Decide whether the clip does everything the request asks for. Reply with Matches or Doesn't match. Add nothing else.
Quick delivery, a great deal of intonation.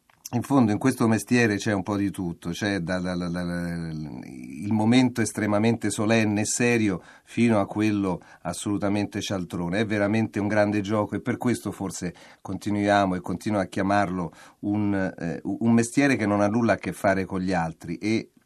Doesn't match